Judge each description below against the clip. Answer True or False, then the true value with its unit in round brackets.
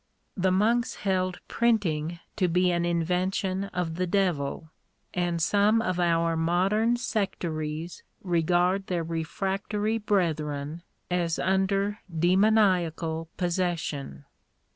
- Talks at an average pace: False (105 wpm)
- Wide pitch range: False (2.9 semitones)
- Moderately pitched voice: True (180 Hz)